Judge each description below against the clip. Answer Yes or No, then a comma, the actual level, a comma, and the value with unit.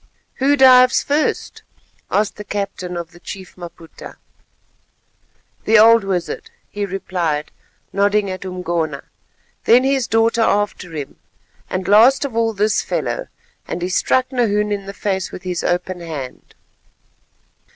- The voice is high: Yes, high, 200 Hz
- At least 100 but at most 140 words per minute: Yes, slow, 135 wpm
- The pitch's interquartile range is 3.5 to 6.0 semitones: Yes, average, 4.2 semitones